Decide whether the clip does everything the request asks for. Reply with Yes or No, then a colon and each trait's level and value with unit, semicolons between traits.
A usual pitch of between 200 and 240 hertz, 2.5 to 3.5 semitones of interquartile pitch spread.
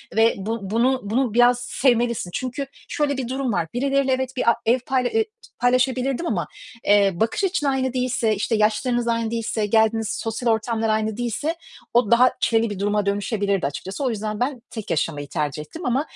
Yes: high, 235 Hz; average, 3.2 semitones